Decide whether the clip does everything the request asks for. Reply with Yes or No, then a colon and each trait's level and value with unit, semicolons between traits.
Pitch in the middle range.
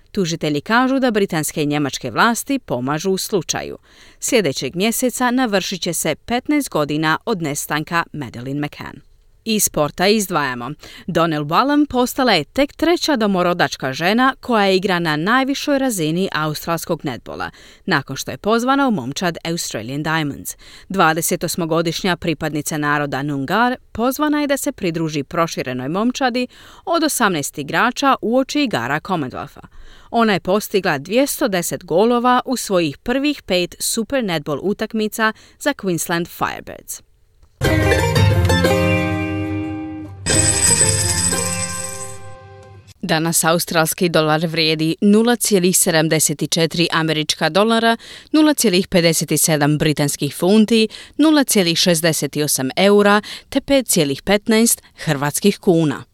Yes: medium, 170 Hz